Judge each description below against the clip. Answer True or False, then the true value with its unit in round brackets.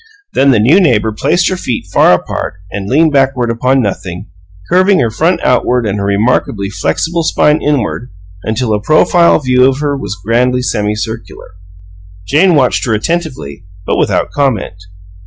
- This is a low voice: True (125 Hz)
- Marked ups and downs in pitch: True (5.9 semitones)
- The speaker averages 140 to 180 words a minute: True (155 wpm)